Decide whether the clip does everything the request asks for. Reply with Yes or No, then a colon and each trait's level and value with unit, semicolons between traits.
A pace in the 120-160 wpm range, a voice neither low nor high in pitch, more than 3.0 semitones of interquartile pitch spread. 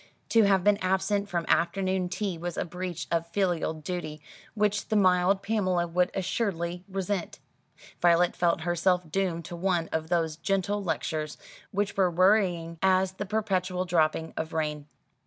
No: average, 155 wpm; medium, 180 Hz; narrow, 2.5 semitones